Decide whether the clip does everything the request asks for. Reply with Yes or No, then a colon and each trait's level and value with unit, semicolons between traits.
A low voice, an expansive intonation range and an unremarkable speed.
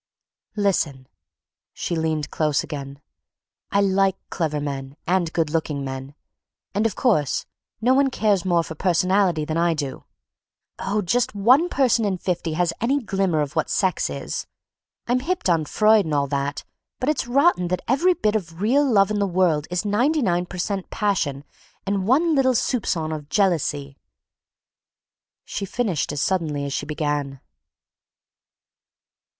No: medium, 180 Hz; wide, 5.7 semitones; average, 155 wpm